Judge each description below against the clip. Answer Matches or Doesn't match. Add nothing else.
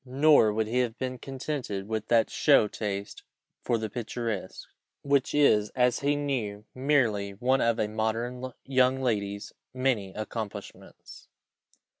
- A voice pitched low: Matches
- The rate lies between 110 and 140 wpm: Matches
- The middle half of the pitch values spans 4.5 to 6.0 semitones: Doesn't match